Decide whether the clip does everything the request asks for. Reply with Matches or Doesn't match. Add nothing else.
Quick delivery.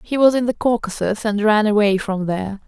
Matches